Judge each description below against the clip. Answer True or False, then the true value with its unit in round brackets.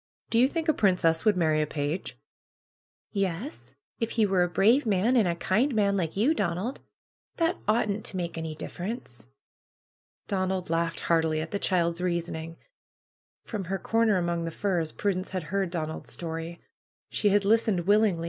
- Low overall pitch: False (185 Hz)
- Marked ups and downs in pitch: False (4.2 semitones)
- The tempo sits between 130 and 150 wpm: False (165 wpm)